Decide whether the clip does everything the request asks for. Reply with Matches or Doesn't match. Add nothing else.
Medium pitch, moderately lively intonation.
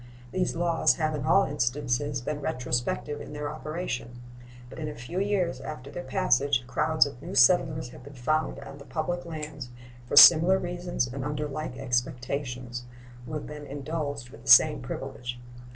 Matches